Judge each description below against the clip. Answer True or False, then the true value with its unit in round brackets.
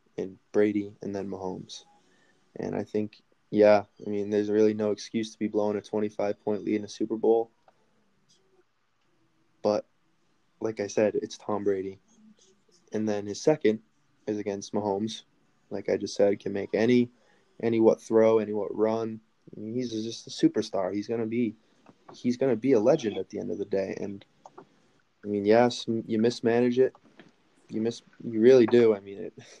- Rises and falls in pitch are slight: True (2.1 semitones)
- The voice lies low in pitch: True (110 Hz)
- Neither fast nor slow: True (175 wpm)